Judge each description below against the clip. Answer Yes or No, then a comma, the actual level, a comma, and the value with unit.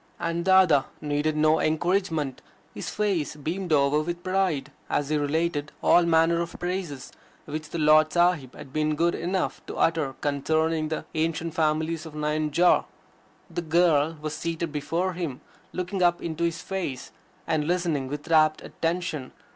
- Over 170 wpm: No, average, 155 wpm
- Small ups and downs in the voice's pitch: Yes, narrow, 2.3 semitones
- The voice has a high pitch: No, medium, 160 Hz